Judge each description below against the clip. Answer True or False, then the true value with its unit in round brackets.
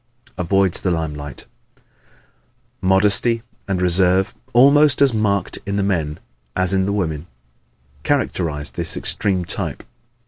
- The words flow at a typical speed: False (125 wpm)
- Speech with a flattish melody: False (3.0 semitones)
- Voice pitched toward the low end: True (95 Hz)